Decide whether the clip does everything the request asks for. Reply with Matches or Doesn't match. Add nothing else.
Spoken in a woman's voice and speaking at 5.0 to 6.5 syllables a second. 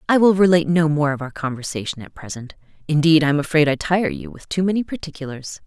Matches